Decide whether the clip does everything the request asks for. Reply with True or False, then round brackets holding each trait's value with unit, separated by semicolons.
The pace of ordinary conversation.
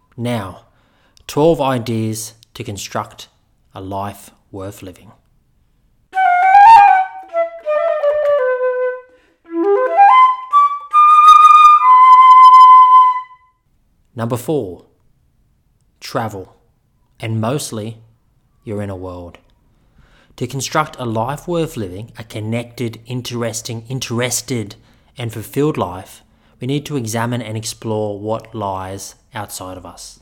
False (80 wpm)